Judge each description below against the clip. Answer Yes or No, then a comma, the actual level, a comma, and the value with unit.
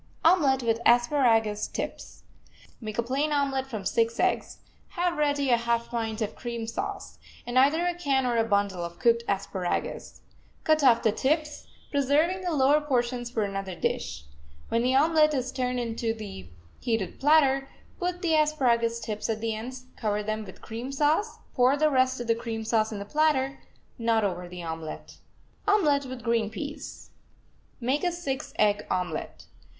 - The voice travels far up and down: No, average, 4.5 semitones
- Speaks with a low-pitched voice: No, high, 245 Hz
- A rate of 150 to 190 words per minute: Yes, average, 170 wpm